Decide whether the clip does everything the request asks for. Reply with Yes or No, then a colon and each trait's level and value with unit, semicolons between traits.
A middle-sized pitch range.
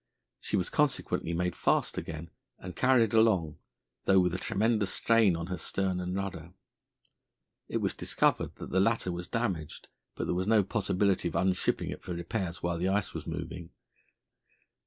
Yes: average, 3.1 semitones